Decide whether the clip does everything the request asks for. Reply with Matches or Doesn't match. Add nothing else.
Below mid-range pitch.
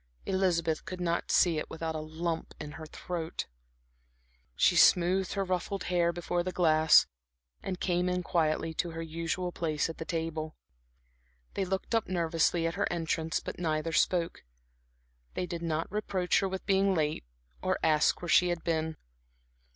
Doesn't match